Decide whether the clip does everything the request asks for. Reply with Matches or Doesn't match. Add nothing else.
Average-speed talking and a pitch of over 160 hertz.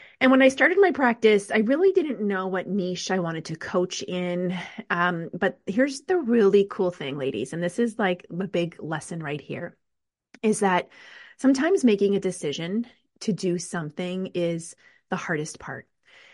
Matches